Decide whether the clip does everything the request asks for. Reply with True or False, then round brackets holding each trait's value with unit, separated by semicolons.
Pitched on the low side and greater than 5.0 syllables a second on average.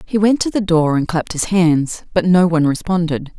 False (175 Hz; 5.4 syllables/s)